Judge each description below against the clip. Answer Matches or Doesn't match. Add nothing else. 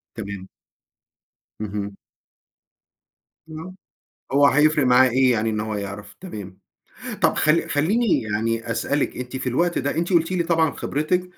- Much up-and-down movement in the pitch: Matches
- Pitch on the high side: Doesn't match